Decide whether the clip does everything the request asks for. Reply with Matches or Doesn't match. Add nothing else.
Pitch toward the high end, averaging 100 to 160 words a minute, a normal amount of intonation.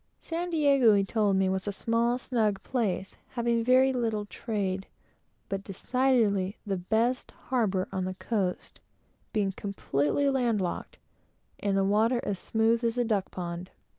Matches